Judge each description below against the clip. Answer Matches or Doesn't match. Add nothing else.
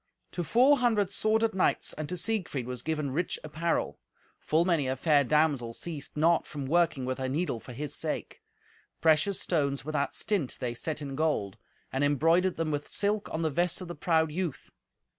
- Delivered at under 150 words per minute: Doesn't match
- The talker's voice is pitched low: Doesn't match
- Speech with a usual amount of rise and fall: Matches